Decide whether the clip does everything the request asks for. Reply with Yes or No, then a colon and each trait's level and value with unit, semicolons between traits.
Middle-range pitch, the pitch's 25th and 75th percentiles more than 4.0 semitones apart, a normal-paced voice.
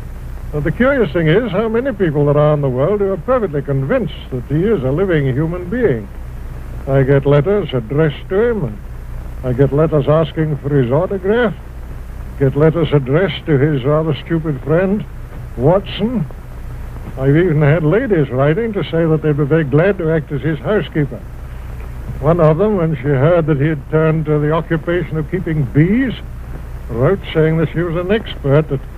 No: medium, 150 Hz; average, 3.5 semitones; average, 180 wpm